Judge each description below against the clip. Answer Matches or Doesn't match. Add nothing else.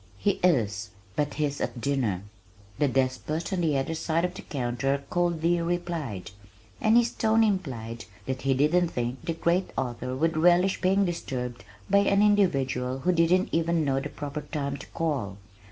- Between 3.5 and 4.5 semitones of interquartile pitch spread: Doesn't match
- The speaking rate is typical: Matches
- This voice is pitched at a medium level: Matches